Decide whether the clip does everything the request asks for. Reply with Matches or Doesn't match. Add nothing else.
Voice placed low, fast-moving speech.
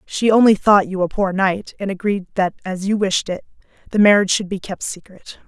Doesn't match